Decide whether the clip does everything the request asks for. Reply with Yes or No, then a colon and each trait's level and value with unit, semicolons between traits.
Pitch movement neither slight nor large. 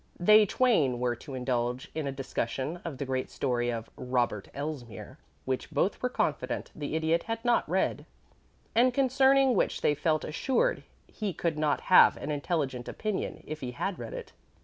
No: wide, 8.7 semitones